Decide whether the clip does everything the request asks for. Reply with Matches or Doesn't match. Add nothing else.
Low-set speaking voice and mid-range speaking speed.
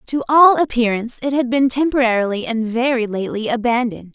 Doesn't match